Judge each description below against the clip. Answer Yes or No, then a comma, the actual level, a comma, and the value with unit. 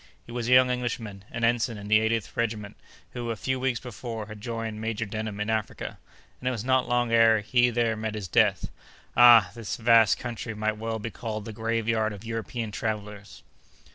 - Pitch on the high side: No, low, 115 Hz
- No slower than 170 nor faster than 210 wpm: Yes, average, 200 wpm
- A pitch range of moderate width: No, narrow, 1.7 semitones